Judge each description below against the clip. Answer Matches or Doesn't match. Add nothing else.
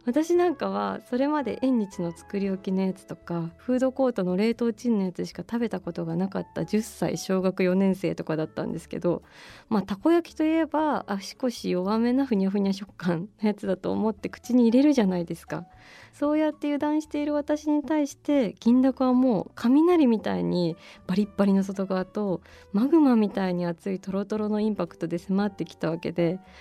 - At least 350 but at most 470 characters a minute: Matches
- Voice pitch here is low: Doesn't match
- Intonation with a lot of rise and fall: Matches